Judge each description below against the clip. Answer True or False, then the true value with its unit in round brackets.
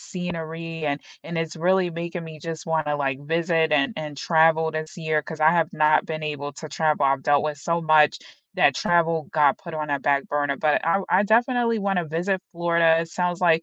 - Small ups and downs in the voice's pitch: True (2.0 semitones)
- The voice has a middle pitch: True (160 Hz)